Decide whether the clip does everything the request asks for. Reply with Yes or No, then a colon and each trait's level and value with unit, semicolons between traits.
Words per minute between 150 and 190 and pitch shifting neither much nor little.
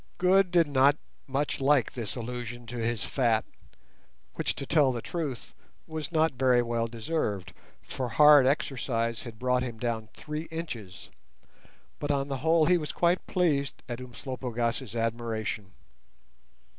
No: average, 140 wpm; average, 4.1 semitones